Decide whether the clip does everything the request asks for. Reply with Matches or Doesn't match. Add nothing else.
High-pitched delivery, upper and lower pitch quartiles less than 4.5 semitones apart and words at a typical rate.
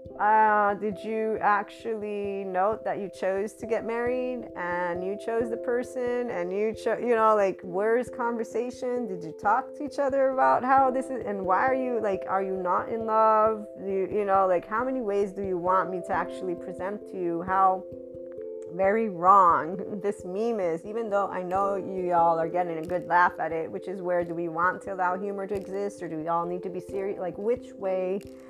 Doesn't match